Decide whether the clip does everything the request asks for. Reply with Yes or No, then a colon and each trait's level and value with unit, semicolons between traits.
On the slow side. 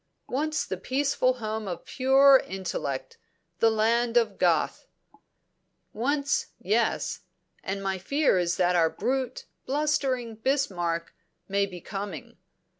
Yes: slow, 115 wpm